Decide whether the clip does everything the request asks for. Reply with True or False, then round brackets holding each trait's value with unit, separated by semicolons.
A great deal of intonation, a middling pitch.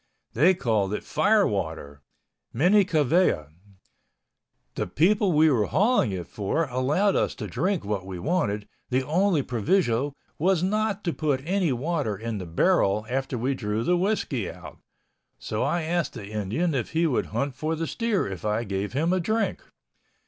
True (9.0 semitones; 145 Hz)